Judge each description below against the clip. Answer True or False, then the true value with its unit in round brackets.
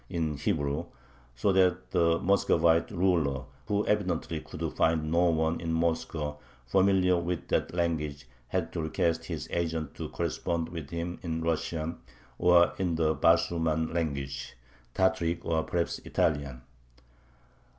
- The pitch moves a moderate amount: False (1.9 semitones)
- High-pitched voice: False (85 Hz)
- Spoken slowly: True (130 wpm)